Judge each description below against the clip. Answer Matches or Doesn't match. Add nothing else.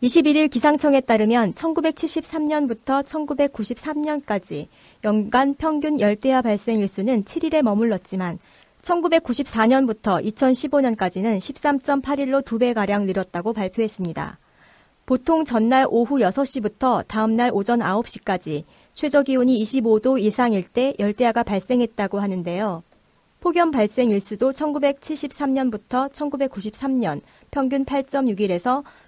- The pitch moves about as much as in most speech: Matches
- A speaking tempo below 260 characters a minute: Matches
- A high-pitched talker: Matches